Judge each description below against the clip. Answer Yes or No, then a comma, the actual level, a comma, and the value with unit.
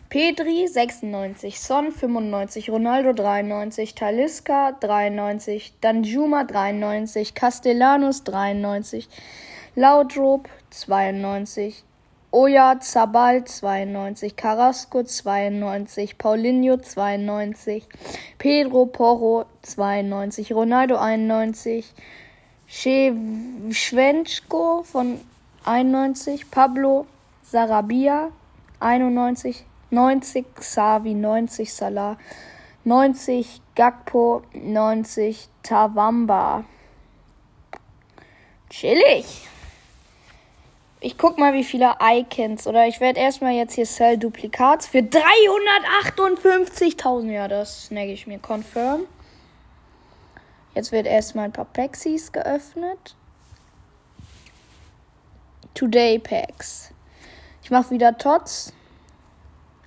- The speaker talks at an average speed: No, slow, 75 wpm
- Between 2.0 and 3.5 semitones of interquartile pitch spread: No, average, 4.0 semitones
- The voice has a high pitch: Yes, high, 235 Hz